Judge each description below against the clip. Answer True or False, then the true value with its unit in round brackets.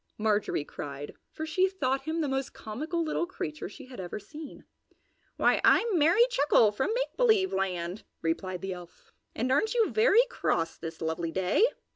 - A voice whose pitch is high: True (270 Hz)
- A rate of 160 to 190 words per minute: True (170 wpm)